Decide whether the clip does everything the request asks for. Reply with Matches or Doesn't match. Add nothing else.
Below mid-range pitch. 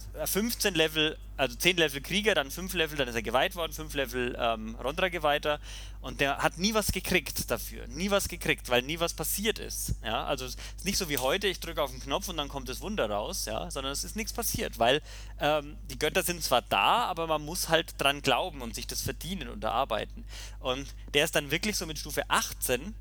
Doesn't match